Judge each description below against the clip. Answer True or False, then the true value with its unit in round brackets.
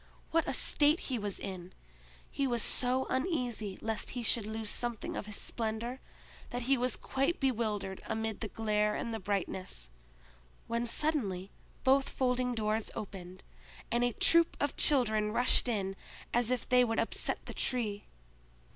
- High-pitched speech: True (230 Hz)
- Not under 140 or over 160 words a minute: True (155 wpm)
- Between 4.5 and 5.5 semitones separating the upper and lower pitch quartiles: False (3.2 semitones)